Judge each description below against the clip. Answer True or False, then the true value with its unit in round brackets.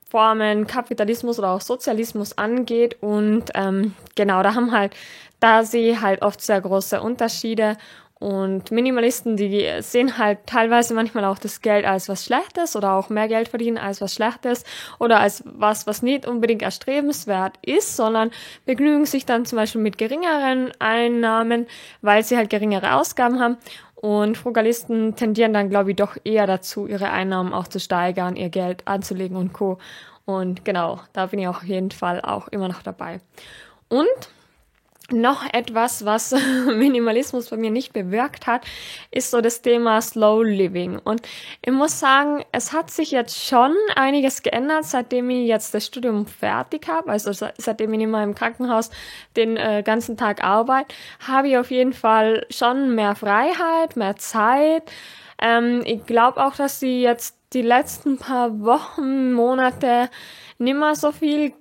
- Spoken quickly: False (160 wpm)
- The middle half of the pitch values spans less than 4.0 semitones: True (3.3 semitones)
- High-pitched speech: True (230 Hz)